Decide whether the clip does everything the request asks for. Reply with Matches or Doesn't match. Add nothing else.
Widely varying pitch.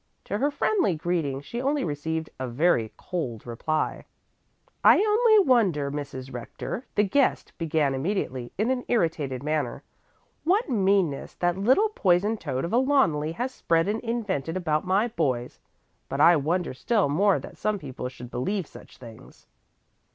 Matches